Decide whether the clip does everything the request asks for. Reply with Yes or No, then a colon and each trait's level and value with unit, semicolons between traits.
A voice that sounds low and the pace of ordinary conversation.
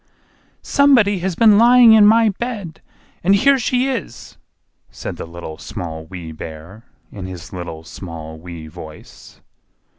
No: low, 105 Hz; slow, 130 wpm